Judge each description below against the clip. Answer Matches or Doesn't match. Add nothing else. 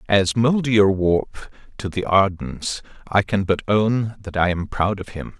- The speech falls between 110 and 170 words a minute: Matches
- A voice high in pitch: Doesn't match